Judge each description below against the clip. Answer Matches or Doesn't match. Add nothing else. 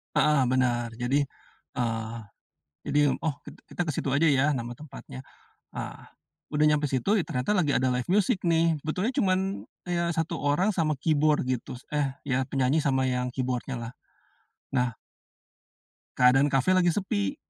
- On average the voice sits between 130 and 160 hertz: Matches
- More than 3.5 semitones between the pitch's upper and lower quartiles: Matches